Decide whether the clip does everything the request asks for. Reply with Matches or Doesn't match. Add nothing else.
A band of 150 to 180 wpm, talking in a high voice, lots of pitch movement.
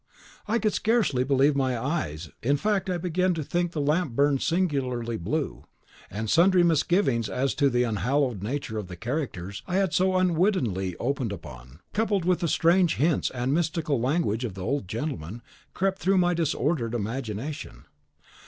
Doesn't match